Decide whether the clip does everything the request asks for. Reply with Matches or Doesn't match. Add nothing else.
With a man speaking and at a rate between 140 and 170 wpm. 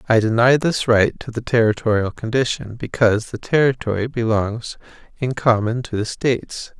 Matches